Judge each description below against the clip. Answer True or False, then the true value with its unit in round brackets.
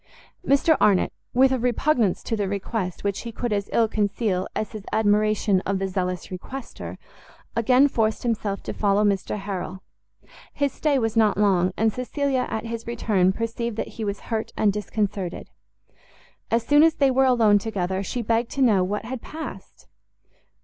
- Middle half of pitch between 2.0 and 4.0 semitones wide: True (3.3 semitones)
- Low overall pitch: False (220 Hz)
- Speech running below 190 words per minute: True (170 wpm)